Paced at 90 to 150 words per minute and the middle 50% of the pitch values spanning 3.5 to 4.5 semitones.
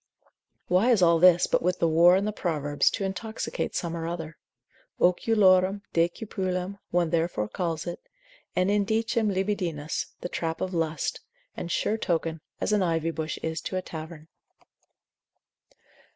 No: average, 145 wpm; average, 2.9 semitones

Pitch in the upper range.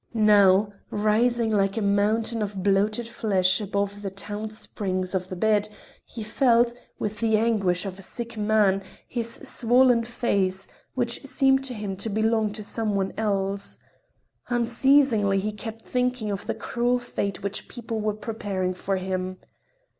Yes: high, 215 Hz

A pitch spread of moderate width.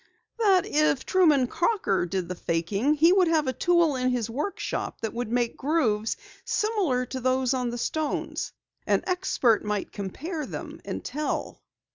No: wide, 6.3 semitones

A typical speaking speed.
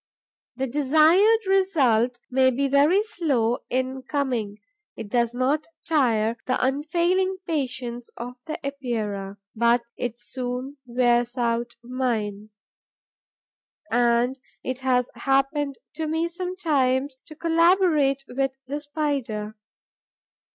No: slow, 110 wpm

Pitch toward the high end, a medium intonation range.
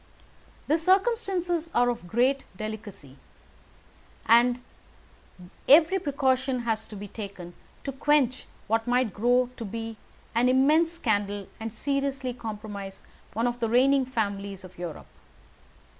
Yes: high, 240 Hz; average, 4.4 semitones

